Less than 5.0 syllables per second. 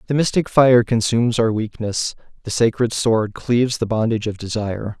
No: 5.3 syllables/s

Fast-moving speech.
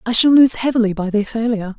Yes: fast, 235 wpm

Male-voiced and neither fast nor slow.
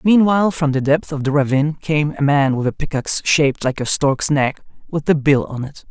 No: male; fast, 235 wpm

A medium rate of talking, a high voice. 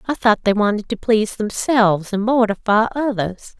Yes: average, 165 wpm; high, 215 Hz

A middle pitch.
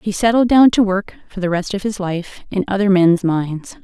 No: high, 200 Hz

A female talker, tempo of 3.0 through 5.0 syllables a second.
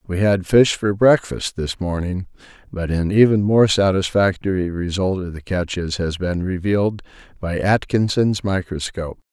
No: male; 4.6 syllables/s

